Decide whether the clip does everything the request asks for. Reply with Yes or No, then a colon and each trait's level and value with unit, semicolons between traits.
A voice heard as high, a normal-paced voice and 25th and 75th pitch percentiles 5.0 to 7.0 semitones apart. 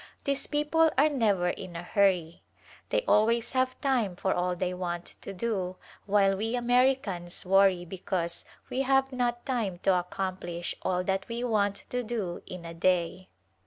Yes: high, 195 Hz; average, 170 wpm; wide, 5.4 semitones